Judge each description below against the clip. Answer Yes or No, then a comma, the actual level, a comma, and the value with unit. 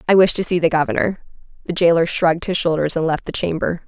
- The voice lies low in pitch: No, medium, 170 Hz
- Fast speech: Yes, fast, 230 wpm